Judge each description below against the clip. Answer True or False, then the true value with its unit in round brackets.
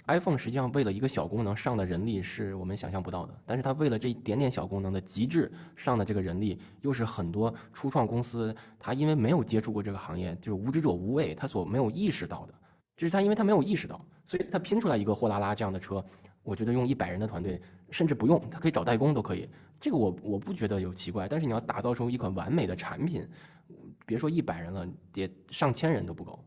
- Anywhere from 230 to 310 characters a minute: False (385 characters per minute)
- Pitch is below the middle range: True (110 Hz)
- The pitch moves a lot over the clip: True (6.7 semitones)